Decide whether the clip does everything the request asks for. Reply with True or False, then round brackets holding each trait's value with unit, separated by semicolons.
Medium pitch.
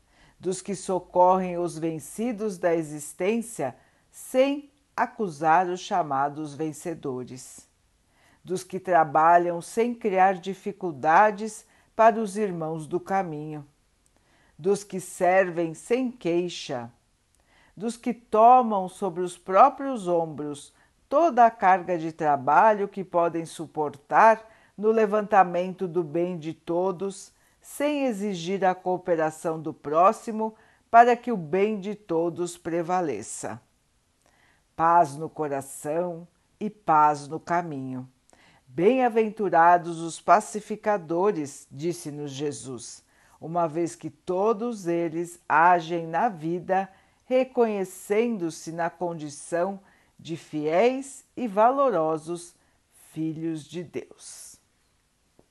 True (175 Hz)